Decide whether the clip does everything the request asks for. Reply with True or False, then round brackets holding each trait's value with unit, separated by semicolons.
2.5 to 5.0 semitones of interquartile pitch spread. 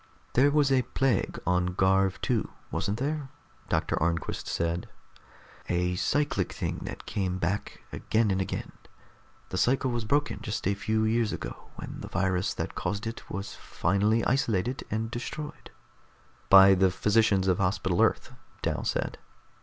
True (4.3 semitones)